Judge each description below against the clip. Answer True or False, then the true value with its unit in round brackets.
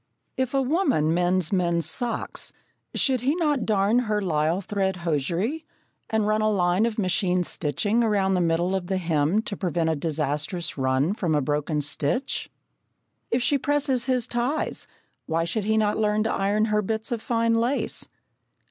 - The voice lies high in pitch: True (200 Hz)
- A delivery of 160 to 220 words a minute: True (170 wpm)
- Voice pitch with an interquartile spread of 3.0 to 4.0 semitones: False (5.4 semitones)